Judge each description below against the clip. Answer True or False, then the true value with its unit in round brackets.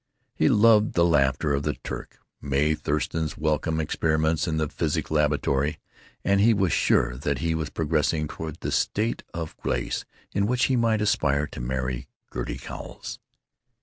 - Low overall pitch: True (80 Hz)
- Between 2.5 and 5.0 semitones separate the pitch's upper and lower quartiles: True (3.2 semitones)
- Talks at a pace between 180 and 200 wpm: False (160 wpm)